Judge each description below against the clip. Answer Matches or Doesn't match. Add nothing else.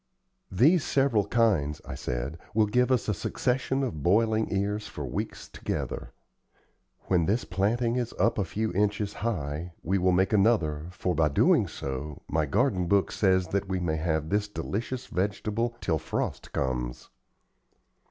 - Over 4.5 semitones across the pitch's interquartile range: Matches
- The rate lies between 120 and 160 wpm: Matches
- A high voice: Doesn't match